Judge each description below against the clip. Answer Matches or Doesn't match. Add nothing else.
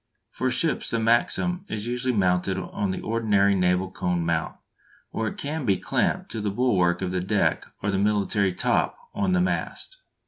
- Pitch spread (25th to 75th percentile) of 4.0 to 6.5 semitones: Matches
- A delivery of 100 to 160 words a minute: Doesn't match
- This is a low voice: Matches